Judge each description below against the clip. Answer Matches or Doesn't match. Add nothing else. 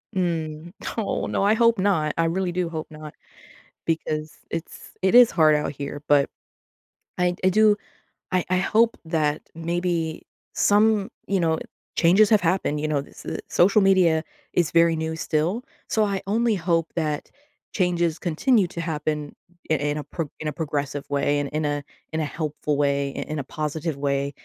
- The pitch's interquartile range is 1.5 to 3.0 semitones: Doesn't match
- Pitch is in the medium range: Matches